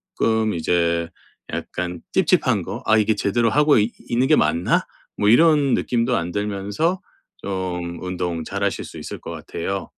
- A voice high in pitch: No, low, 100 Hz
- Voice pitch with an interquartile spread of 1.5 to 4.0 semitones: No, average, 5.1 semitones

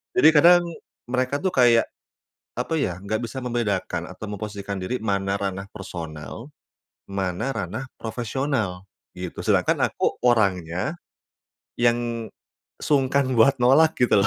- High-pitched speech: No, low, 115 Hz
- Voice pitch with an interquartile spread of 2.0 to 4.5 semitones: No, average, 5.0 semitones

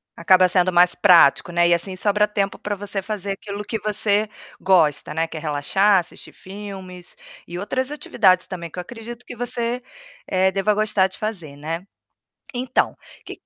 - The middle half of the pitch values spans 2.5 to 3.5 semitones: Yes, average, 3.0 semitones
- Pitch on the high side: Yes, high, 195 Hz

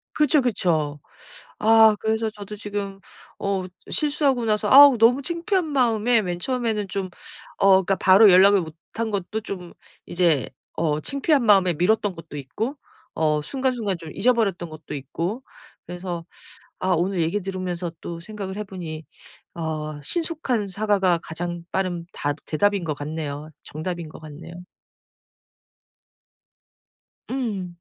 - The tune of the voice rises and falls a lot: No, average, 4.8 semitones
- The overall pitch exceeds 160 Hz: Yes, high, 190 Hz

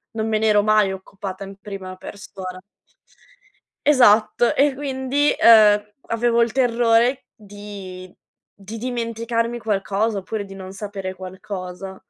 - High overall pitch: Yes, high, 210 Hz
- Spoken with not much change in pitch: No, average, 3.1 semitones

